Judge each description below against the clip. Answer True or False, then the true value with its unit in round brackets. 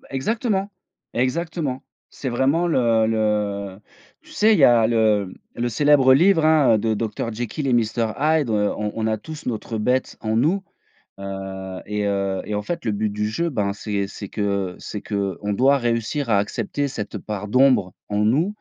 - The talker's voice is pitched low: True (115 Hz)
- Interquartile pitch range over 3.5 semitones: True (5.2 semitones)